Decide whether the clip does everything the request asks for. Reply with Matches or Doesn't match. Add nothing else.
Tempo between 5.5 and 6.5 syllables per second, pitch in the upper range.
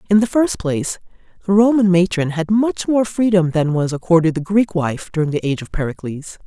Doesn't match